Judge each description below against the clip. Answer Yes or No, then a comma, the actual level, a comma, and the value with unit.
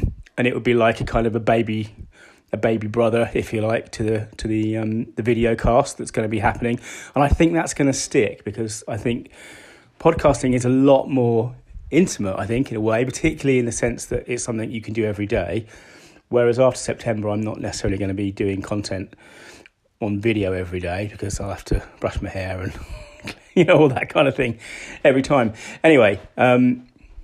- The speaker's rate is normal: No, fast, 210 wpm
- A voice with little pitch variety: No, average, 3.0 semitones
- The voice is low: Yes, low, 115 Hz